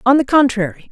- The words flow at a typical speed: Yes, average, 195 wpm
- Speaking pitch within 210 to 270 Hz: Yes, very high, 260 Hz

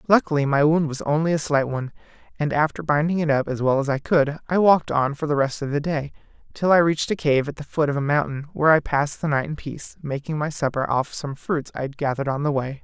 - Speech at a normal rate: No, fast, 265 wpm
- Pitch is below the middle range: No, medium, 145 Hz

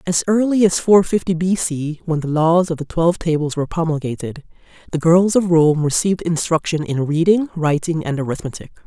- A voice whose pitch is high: No, medium, 165 Hz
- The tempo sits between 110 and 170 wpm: No, average, 185 wpm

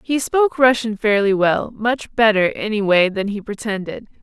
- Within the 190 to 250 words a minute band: No, average, 155 wpm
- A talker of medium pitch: No, high, 215 Hz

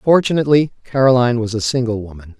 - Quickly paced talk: No, average, 150 wpm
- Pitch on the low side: Yes, low, 120 Hz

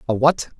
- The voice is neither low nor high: No, low, 130 Hz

